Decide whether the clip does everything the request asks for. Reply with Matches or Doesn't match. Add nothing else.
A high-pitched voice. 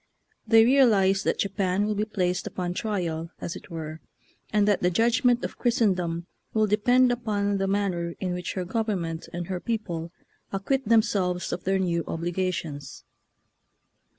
Matches